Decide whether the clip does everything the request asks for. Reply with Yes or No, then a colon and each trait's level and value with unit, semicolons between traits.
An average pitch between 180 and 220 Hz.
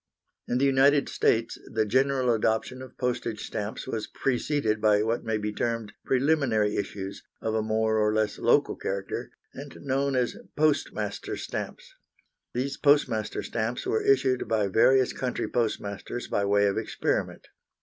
No: low, 115 Hz